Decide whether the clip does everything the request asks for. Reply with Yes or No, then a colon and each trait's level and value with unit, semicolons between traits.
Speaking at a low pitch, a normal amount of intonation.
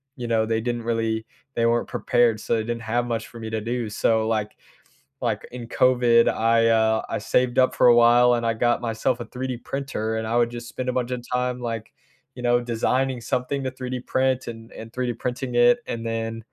No: low, 120 Hz; narrow, 1.7 semitones